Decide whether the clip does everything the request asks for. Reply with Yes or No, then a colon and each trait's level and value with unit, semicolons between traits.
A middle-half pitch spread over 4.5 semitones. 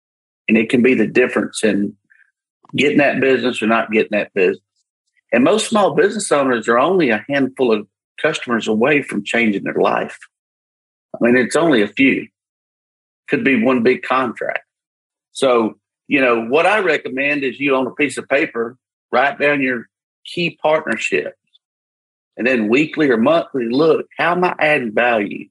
Yes: average, 5.1 semitones